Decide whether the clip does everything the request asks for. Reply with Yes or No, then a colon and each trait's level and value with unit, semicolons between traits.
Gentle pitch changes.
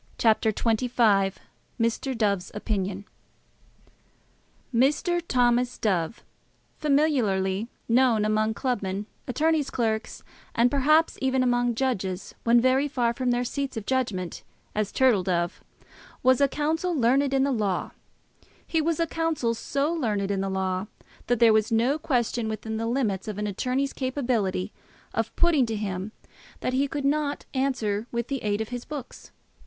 No: average, 4.4 semitones